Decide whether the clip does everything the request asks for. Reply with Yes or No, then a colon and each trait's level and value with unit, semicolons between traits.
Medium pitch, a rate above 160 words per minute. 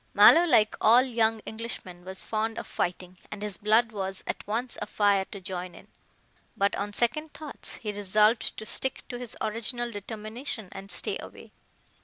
No: high, 215 Hz; average, 170 wpm